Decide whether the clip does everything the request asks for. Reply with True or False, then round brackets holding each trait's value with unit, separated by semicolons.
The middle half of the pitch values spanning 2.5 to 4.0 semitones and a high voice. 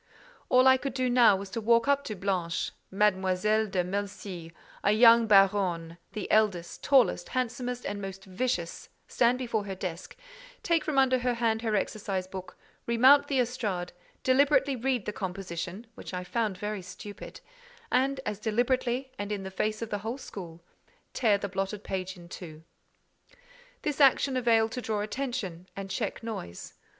False (4.6 semitones; 215 Hz)